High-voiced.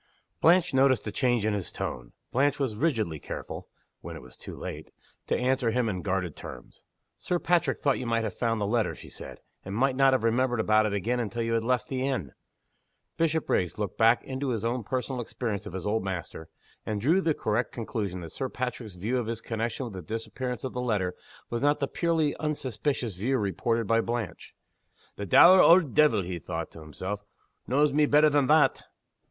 No: low, 115 Hz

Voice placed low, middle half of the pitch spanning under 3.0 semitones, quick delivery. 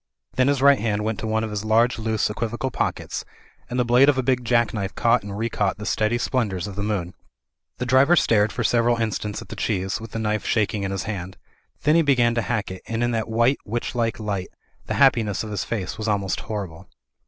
Yes: low, 110 Hz; narrow, 2.6 semitones; fast, 235 wpm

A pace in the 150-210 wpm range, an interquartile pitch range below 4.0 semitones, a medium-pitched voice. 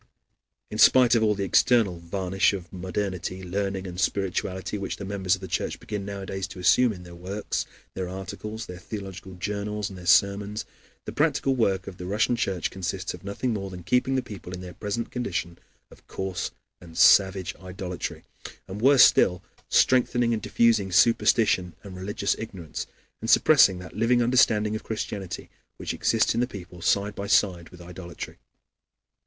No: average, 170 wpm; average, 2.7 semitones; very low, 95 Hz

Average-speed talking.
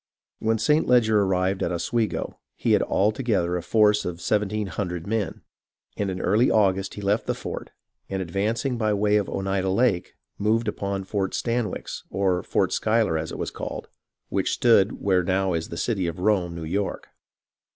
Yes: average, 180 wpm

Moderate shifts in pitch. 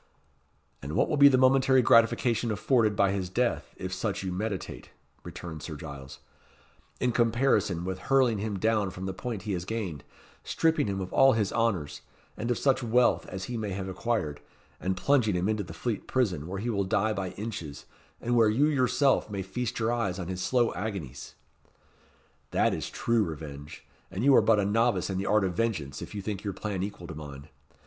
Yes: average, 4.2 semitones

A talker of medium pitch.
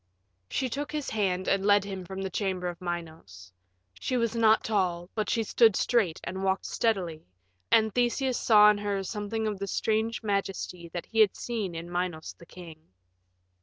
No: high, 195 Hz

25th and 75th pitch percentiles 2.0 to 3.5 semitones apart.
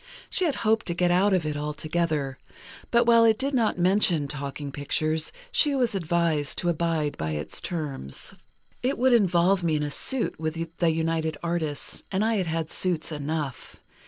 No: average, 4.8 semitones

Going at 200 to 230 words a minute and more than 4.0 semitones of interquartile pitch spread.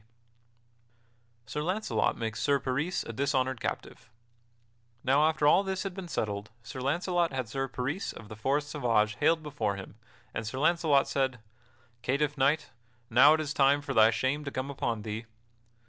No: average, 170 wpm; average, 4.5 semitones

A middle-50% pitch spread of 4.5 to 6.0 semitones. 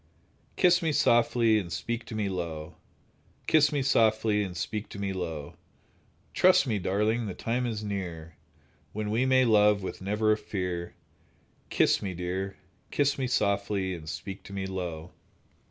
No: average, 3.8 semitones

